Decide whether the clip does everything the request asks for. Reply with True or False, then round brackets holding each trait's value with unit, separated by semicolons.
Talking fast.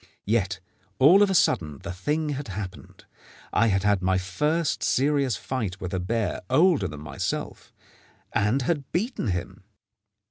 False (150 wpm)